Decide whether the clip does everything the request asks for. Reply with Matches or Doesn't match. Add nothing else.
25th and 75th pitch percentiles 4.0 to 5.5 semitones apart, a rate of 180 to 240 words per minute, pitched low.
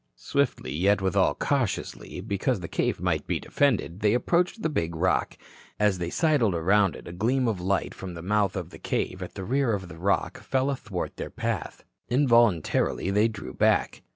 Matches